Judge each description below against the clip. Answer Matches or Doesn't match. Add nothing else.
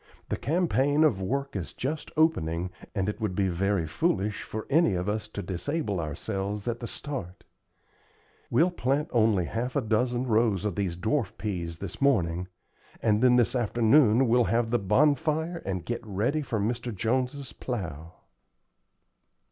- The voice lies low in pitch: Matches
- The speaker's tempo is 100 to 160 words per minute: Matches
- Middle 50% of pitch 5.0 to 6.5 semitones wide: Matches